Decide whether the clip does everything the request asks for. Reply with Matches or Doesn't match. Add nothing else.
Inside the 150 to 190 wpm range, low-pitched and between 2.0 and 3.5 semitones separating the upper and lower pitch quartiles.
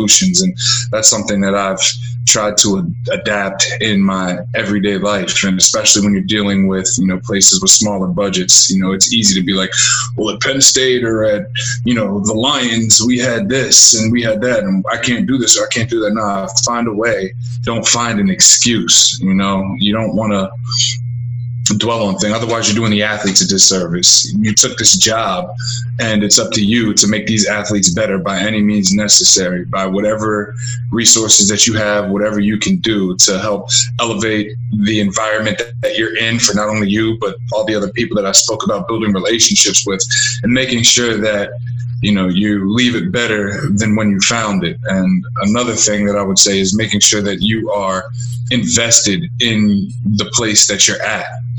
Doesn't match